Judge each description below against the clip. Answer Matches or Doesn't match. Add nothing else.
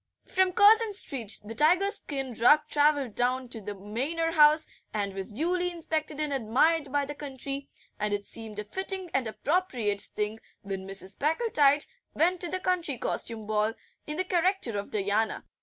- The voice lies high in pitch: Matches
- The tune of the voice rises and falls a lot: Matches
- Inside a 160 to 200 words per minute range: Matches